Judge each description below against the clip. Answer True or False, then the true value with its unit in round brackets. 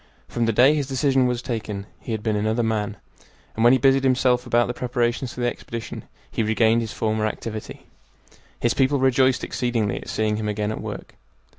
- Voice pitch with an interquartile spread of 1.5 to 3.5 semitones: True (2.6 semitones)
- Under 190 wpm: False (195 wpm)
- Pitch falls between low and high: False (120 Hz)